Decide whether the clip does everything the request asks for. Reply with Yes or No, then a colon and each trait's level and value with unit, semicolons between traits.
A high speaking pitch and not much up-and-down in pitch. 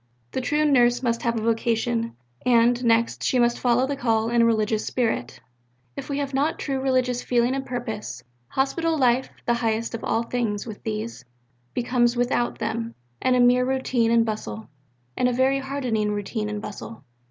Yes: high, 240 Hz; narrow, 2.1 semitones